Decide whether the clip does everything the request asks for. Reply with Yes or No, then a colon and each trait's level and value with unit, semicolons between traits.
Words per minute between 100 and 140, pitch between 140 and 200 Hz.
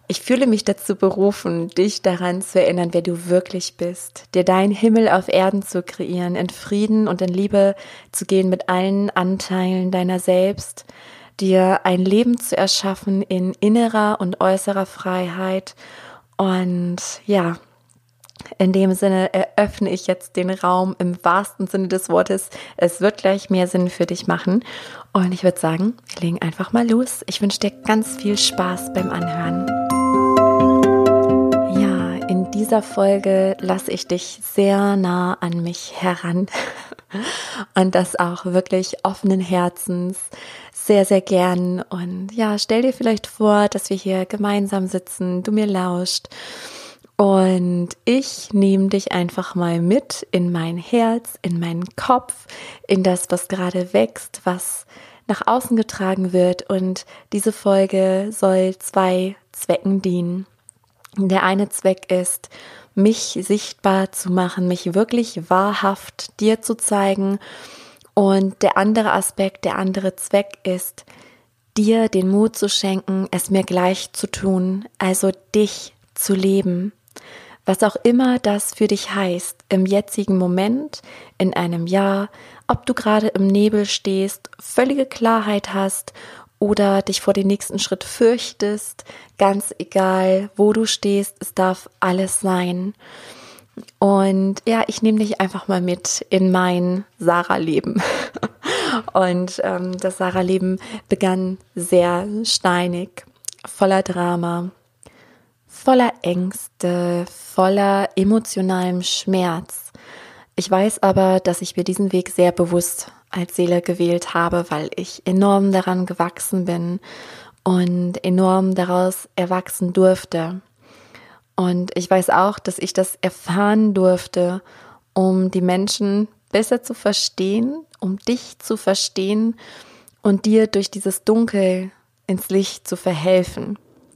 Yes: average, 135 wpm; high, 190 Hz